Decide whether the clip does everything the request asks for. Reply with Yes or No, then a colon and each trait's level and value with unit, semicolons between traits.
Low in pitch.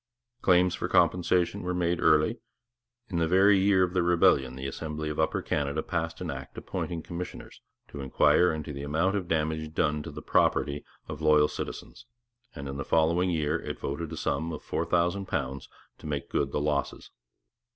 Yes: very low, 80 Hz